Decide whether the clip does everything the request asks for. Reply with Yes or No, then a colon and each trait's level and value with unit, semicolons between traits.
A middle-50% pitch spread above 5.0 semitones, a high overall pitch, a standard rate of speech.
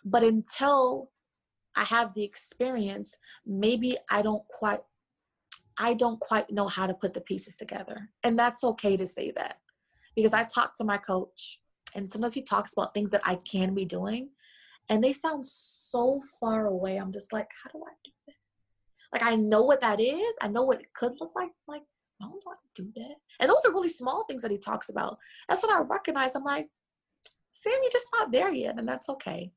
No: wide, 5.6 semitones; high, 235 Hz; fast, 215 wpm